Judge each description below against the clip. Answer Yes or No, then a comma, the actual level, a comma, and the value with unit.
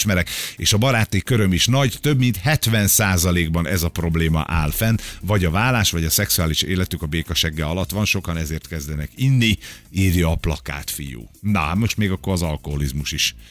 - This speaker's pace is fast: Yes, fast, 180 wpm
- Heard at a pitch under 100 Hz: Yes, very low, 90 Hz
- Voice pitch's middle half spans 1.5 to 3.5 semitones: No, average, 4.6 semitones